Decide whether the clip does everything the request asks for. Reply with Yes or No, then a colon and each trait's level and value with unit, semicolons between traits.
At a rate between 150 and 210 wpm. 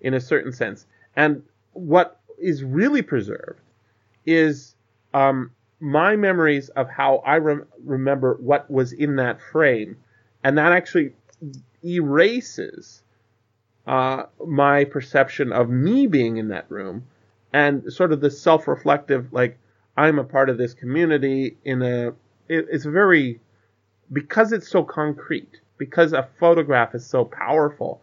No: slow, 135 wpm